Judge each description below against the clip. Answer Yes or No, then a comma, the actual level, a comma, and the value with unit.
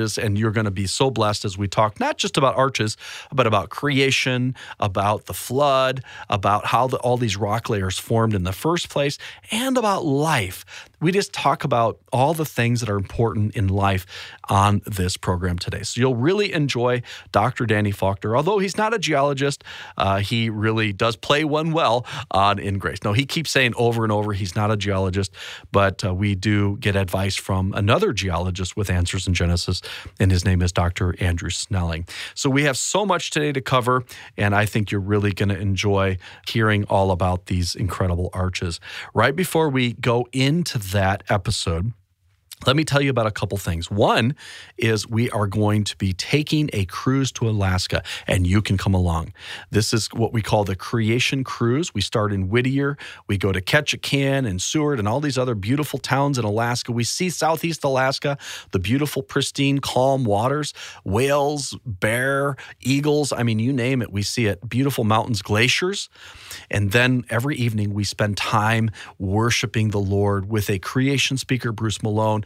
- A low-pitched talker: Yes, low, 110 Hz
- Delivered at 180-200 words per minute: Yes, average, 185 wpm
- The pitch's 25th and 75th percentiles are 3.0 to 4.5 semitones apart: No, average, 5.0 semitones